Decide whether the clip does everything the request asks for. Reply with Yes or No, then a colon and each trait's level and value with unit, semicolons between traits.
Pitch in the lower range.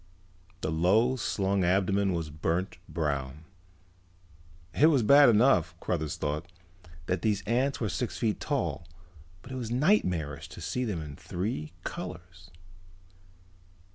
Yes: very low, 95 Hz